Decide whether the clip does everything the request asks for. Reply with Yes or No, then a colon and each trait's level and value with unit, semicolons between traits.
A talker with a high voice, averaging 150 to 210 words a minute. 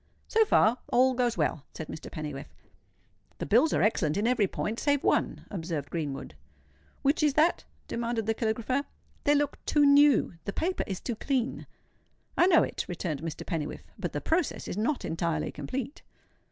Yes: high, 230 Hz; average, 165 wpm